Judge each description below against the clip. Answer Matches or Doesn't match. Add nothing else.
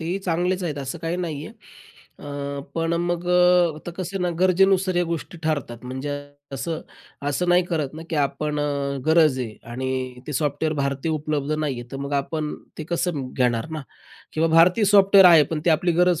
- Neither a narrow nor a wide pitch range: Matches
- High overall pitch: Doesn't match